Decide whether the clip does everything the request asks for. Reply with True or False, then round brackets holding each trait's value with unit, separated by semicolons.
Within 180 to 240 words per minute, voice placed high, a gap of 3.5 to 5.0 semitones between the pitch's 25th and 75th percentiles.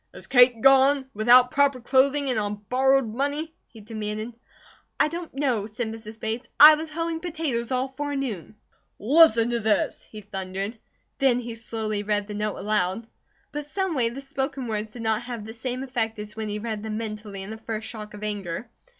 True (185 wpm; 230 Hz; 4.1 semitones)